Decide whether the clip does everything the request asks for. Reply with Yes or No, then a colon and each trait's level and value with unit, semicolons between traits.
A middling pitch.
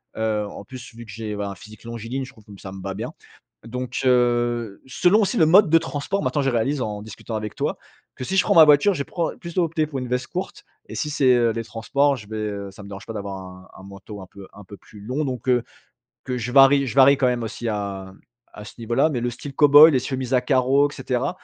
No: low, 120 Hz